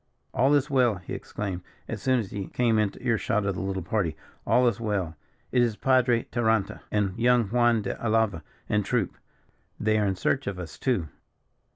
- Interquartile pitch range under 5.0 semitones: Yes, average, 3.8 semitones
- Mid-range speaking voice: No, low, 110 Hz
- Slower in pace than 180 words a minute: No, average, 195 wpm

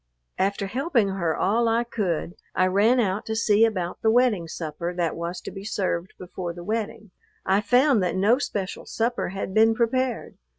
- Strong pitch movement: No, average, 3.9 semitones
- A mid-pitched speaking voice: No, high, 205 Hz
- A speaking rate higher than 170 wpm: Yes, average, 180 wpm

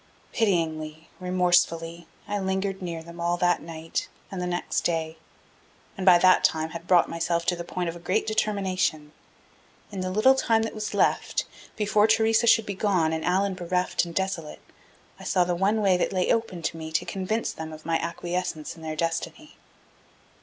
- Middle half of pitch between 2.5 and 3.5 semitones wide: Yes, average, 2.8 semitones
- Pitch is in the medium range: Yes, medium, 180 Hz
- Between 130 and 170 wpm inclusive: No, average, 185 wpm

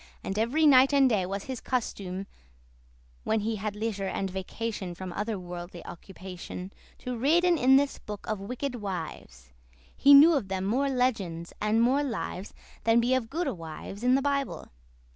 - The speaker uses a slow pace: No, average, 170 wpm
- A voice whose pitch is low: No, high, 220 Hz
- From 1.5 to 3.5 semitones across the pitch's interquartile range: No, wide, 5.5 semitones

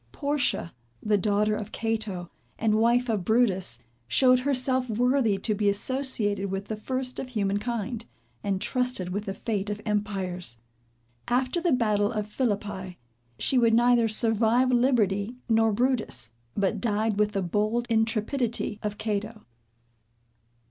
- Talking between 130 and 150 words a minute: Yes, average, 140 wpm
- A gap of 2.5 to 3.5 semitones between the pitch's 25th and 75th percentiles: Yes, average, 3.2 semitones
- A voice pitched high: Yes, high, 220 Hz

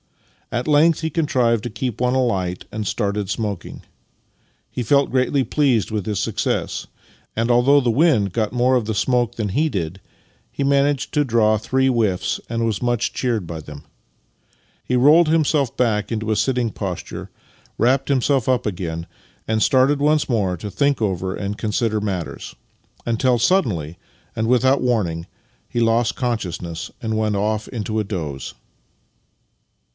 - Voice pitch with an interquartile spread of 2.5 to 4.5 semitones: Yes, average, 4.1 semitones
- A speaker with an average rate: Yes, average, 160 wpm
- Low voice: Yes, low, 115 Hz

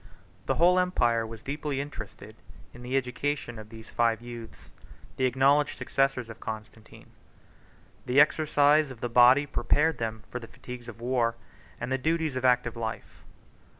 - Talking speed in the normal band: Yes, average, 160 wpm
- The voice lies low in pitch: Yes, low, 125 Hz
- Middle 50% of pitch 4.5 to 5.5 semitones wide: No, average, 3.7 semitones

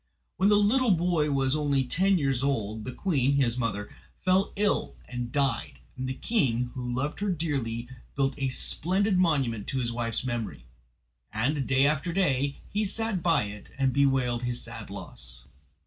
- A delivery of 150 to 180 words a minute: Yes, average, 170 wpm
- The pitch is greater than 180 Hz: No, low, 135 Hz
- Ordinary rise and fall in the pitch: No, wide, 5.9 semitones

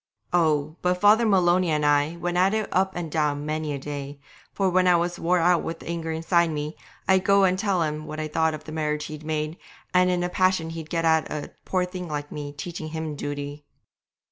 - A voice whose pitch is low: No, medium, 165 Hz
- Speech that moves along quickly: Yes, fast, 225 wpm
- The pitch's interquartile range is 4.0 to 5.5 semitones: No, average, 2.9 semitones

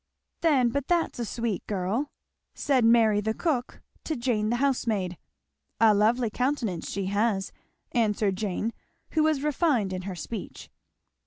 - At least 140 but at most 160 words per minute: Yes, average, 145 wpm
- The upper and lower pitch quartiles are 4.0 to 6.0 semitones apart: Yes, average, 4.4 semitones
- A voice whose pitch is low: No, high, 230 Hz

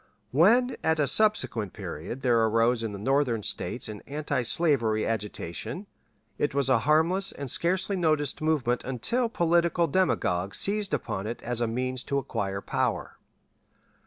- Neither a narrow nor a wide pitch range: No, wide, 6.7 semitones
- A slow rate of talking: No, average, 145 wpm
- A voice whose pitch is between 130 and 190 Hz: Yes, low, 135 Hz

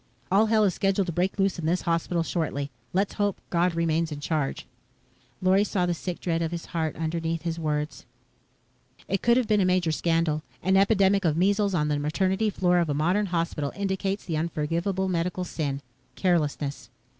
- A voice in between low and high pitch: Yes, medium, 175 Hz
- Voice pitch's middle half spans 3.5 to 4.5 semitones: No, average, 3.1 semitones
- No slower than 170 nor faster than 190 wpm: Yes, average, 185 wpm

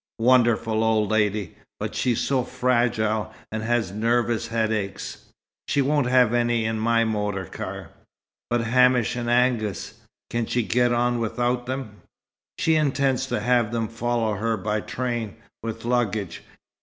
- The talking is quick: No, average, 145 wpm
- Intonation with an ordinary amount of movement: No, narrow, 2.0 semitones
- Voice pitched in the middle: No, low, 115 Hz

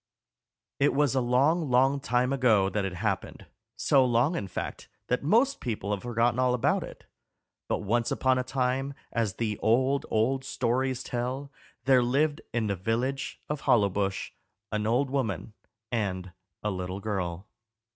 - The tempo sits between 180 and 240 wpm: No, average, 155 wpm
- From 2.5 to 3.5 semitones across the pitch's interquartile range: No, average, 4.1 semitones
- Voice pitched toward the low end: Yes, low, 120 Hz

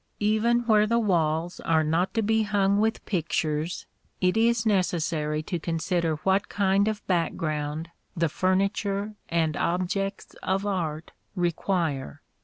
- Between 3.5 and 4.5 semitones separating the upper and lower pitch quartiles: Yes, average, 4.0 semitones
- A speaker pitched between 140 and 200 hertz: Yes, medium, 185 Hz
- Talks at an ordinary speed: No, slow, 130 wpm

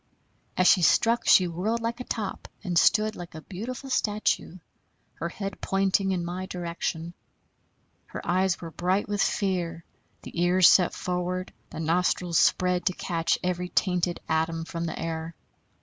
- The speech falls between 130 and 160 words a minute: Yes, average, 155 wpm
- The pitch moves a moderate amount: No, narrow, 2.3 semitones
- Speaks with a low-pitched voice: No, medium, 180 Hz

